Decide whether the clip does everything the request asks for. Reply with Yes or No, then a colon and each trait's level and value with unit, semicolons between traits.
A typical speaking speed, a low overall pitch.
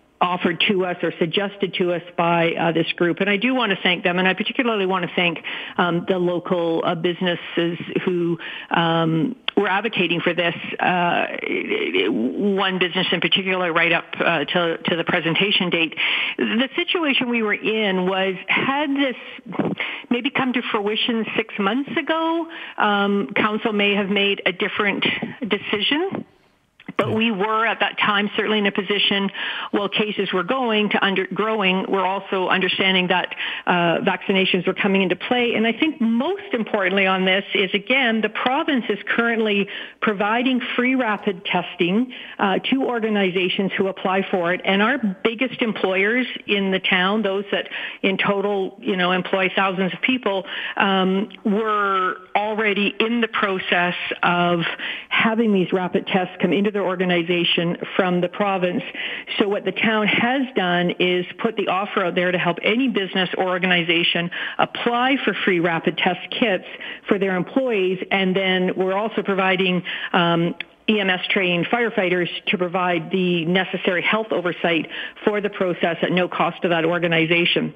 No: average, 160 wpm; high, 195 Hz